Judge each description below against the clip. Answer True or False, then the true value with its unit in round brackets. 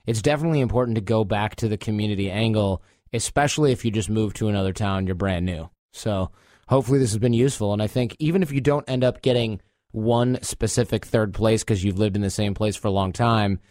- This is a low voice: True (110 Hz)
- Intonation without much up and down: False (3.4 semitones)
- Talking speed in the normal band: False (230 wpm)